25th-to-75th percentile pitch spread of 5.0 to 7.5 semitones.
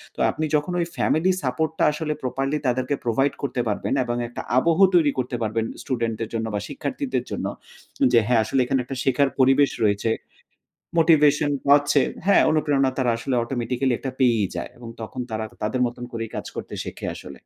No: average, 3.6 semitones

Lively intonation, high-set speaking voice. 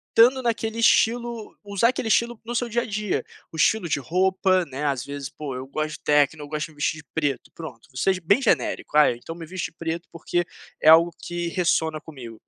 No: wide, 6.0 semitones; medium, 170 Hz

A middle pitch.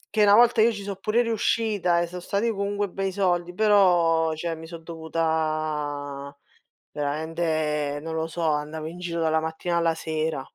Yes: medium, 165 Hz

